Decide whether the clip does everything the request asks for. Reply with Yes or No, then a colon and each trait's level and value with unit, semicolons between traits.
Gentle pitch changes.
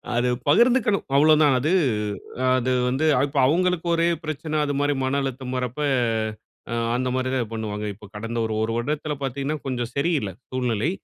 No: average, 3.9 semitones